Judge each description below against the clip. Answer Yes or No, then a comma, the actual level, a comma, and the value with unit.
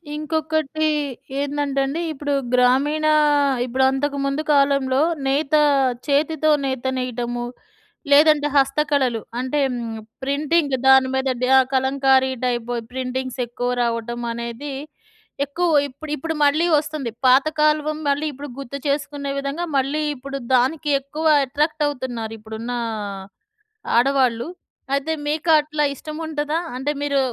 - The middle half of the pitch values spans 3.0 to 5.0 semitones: No, narrow, 2.6 semitones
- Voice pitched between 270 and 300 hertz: Yes, very high, 275 Hz